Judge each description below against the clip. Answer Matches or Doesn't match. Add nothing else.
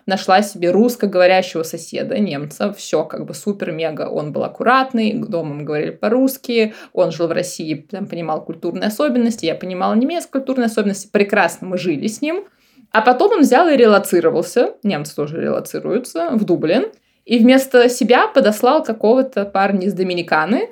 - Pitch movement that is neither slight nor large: Doesn't match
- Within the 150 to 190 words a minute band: Matches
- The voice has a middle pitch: Doesn't match